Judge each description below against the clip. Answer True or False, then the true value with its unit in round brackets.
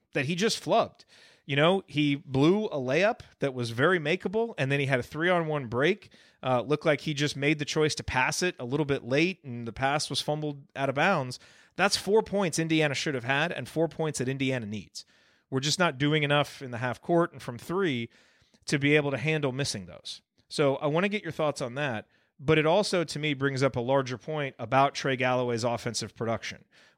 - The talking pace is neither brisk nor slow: False (225 wpm)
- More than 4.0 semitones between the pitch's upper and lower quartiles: False (3.4 semitones)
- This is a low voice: False (145 Hz)